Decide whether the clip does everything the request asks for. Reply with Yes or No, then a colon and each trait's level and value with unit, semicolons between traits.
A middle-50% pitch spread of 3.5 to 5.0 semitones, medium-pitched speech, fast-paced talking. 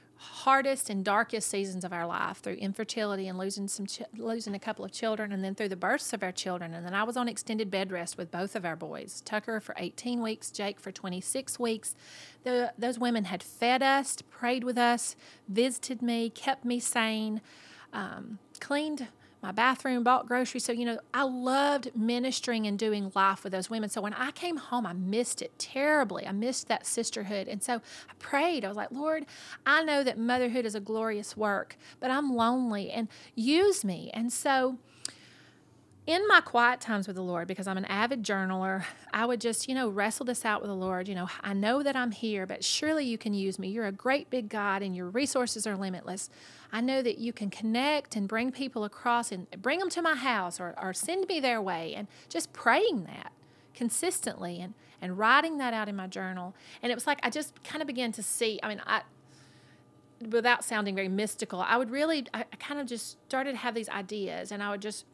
No: average, 4.2 semitones; high, 230 Hz; fast, 215 wpm